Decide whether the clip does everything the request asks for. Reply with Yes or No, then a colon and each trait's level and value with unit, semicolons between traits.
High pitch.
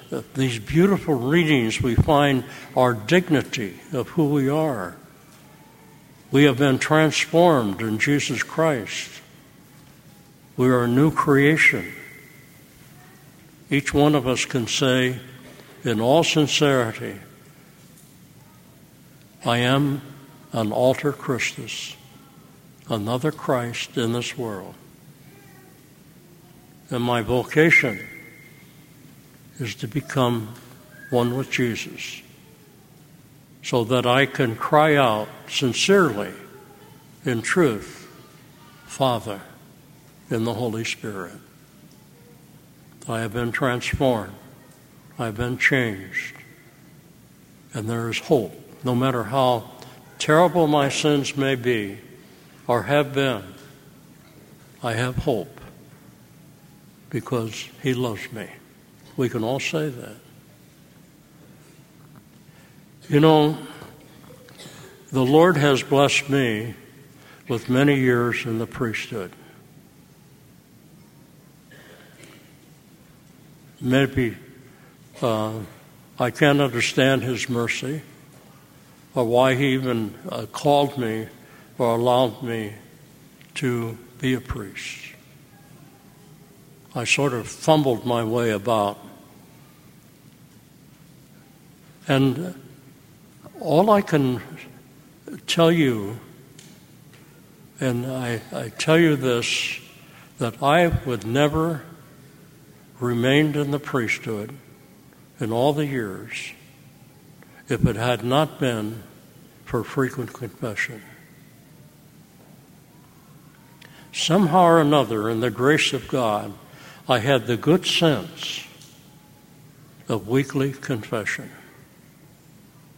No: medium, 140 Hz